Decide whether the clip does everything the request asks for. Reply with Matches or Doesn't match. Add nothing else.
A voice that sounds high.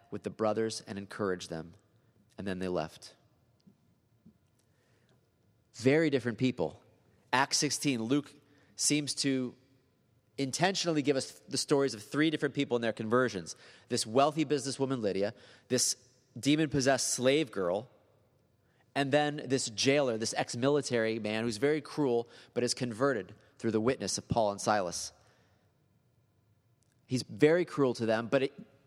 Doesn't match